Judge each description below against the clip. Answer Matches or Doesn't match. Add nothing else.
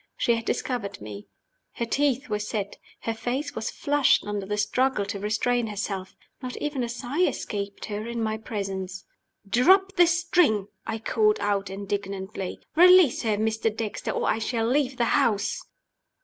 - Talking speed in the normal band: Matches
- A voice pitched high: Matches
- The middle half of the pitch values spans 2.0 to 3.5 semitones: Doesn't match